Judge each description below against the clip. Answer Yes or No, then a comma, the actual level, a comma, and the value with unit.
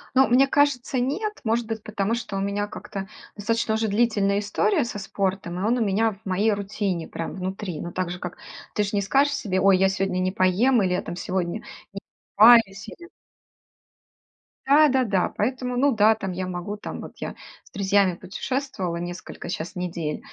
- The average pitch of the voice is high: Yes, high, 205 Hz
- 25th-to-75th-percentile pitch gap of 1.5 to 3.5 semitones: No, average, 3.9 semitones